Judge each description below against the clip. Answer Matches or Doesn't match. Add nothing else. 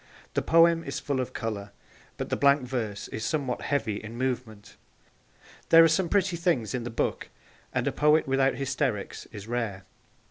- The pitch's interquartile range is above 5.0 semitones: Matches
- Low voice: Matches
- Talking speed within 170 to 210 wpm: Matches